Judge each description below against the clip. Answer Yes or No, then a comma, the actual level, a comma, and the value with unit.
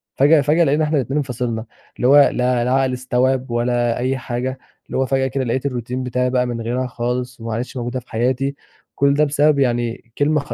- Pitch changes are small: Yes, narrow, 2.1 semitones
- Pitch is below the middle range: Yes, low, 125 Hz